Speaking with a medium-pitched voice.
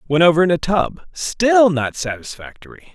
Yes: medium, 155 Hz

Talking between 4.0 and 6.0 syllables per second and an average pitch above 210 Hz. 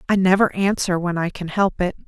No: 5.5 syllables/s; medium, 185 Hz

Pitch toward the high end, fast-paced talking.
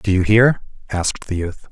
No: low, 100 Hz; fast, 210 wpm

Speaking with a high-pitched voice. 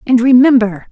Yes: high, 240 Hz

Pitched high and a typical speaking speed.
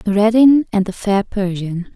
Yes: high, 205 Hz; average, 155 wpm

